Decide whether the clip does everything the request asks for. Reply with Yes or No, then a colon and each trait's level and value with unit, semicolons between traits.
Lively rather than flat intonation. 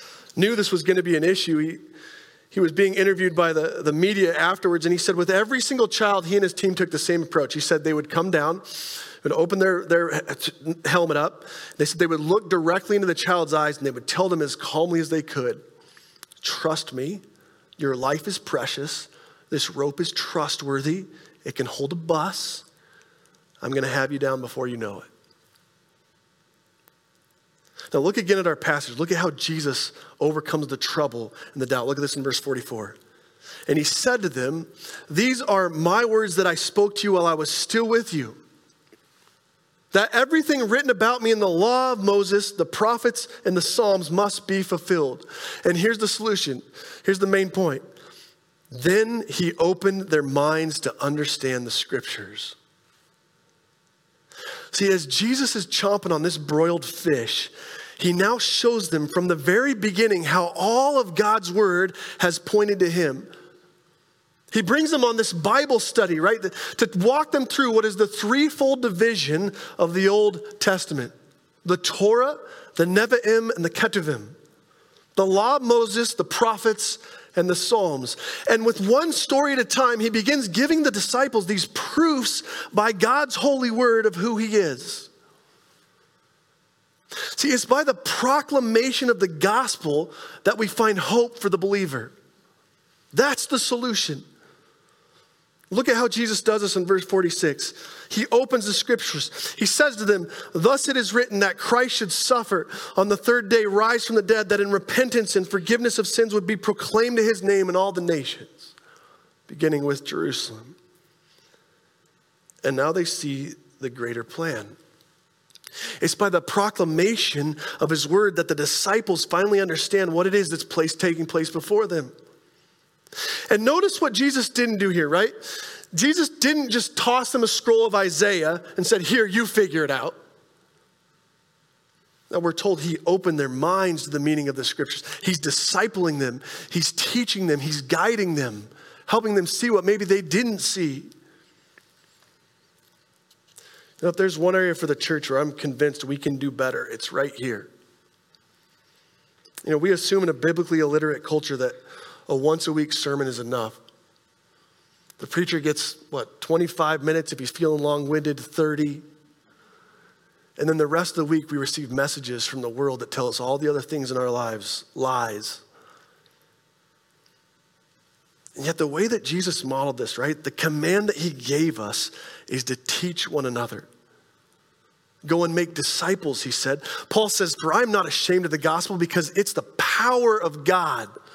Yes: wide, 6.2 semitones